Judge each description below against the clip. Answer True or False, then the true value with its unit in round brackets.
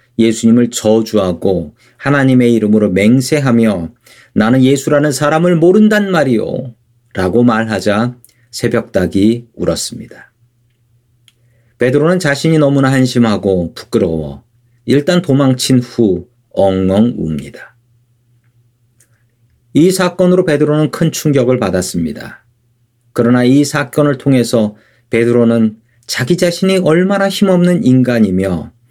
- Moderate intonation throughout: True (3.6 semitones)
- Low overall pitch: True (120 Hz)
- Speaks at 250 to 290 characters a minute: True (260 characters per minute)